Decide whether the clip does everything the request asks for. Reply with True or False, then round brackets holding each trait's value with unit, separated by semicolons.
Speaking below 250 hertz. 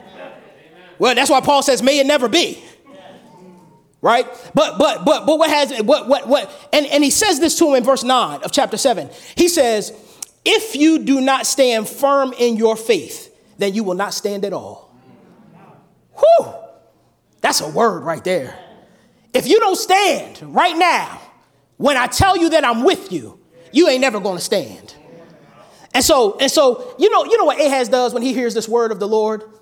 False (275 Hz)